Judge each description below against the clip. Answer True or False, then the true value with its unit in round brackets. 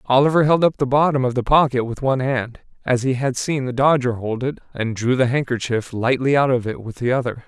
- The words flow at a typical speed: False (240 wpm)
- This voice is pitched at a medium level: False (130 Hz)